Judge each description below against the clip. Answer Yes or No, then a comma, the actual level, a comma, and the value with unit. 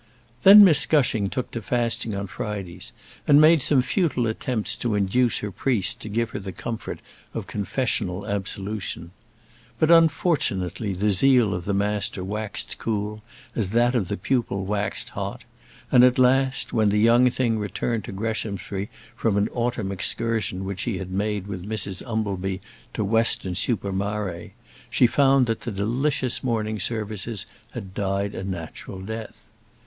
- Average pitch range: Yes, average, 3.6 semitones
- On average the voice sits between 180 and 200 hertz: No, low, 105 Hz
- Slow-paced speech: No, average, 155 wpm